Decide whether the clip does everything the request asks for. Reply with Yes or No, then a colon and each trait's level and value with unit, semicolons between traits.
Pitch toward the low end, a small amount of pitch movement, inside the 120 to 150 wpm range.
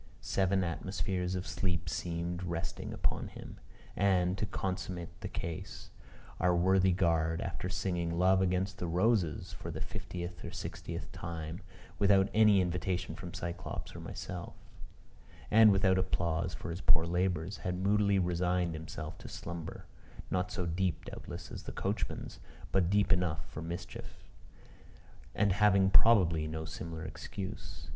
Yes: very low, 90 Hz; narrow, 2.1 semitones; average, 140 wpm